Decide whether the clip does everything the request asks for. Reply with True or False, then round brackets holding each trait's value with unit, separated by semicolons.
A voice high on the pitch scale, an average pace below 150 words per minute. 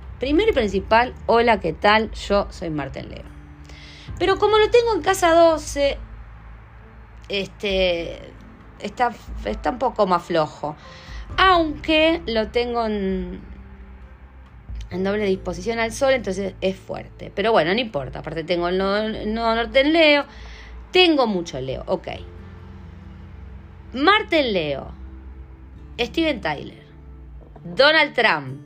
True (195 Hz; 125 wpm)